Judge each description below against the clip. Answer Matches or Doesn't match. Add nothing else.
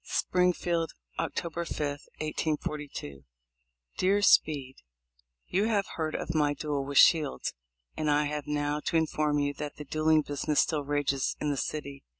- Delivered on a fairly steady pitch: Matches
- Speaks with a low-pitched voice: Doesn't match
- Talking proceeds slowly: Doesn't match